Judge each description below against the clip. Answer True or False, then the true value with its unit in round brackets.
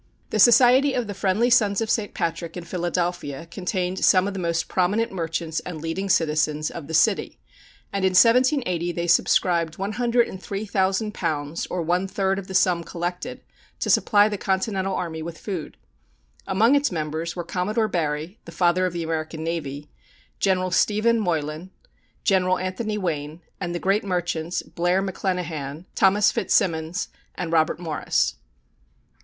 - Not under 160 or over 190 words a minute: False (150 wpm)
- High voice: False (180 Hz)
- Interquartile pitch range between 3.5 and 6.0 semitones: False (3.1 semitones)